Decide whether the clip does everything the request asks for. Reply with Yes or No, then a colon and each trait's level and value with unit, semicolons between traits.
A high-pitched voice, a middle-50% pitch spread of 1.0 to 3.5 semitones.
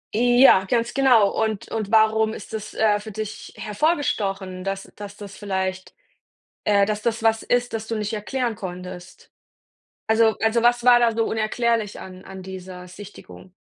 Yes: high, 215 Hz; average, 2.9 semitones